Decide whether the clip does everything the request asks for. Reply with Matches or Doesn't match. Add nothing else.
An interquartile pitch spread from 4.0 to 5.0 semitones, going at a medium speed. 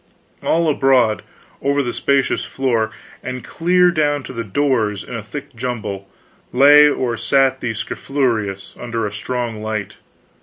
Matches